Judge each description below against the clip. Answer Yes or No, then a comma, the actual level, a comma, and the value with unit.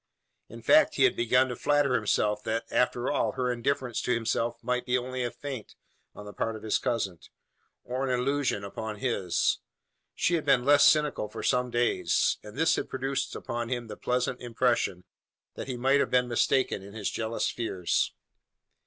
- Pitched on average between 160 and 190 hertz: No, low, 125 Hz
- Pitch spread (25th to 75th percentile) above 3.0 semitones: No, average, 2.7 semitones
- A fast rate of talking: No, average, 185 wpm